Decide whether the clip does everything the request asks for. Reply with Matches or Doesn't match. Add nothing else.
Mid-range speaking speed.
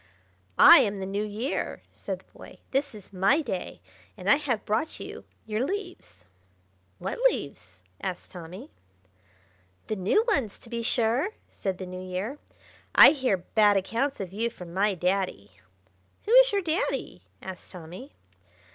Matches